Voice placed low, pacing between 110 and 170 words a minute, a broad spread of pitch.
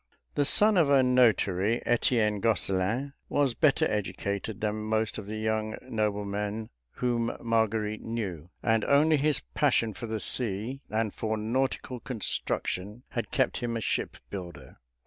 No: low, 110 Hz; average, 140 wpm; average, 3.2 semitones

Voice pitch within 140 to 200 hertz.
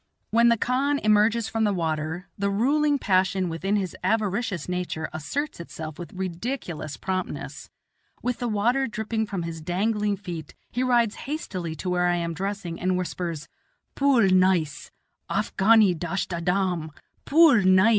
Yes: high, 190 Hz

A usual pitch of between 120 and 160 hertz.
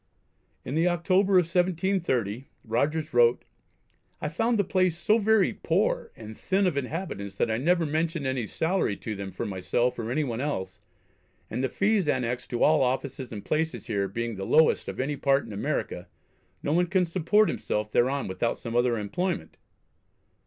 Yes: medium, 140 Hz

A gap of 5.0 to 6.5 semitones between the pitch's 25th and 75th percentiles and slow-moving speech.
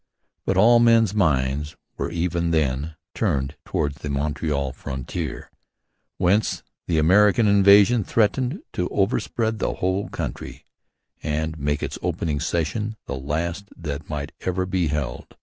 Yes: wide, 5.5 semitones; slow, 130 wpm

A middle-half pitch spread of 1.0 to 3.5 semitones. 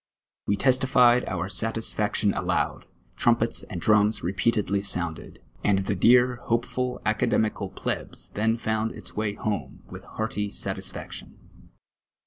Yes: average, 2.8 semitones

